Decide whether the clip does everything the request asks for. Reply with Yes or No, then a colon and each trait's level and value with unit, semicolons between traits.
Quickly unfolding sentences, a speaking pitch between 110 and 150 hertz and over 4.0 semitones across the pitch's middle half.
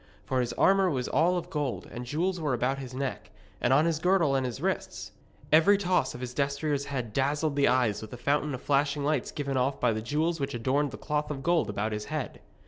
No: fast, 230 wpm; medium, 140 Hz; average, 3.4 semitones